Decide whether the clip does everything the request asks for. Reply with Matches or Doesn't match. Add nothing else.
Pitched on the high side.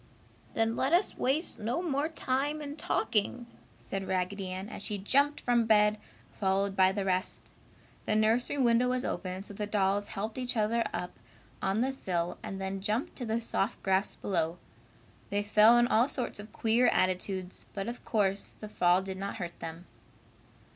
Matches